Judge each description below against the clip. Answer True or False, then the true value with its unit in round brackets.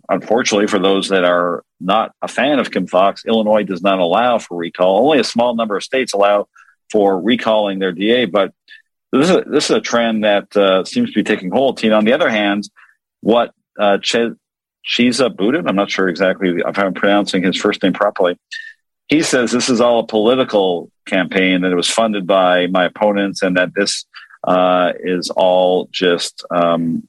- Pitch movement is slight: False (3.5 semitones)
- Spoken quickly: False (190 wpm)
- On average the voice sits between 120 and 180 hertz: False (100 Hz)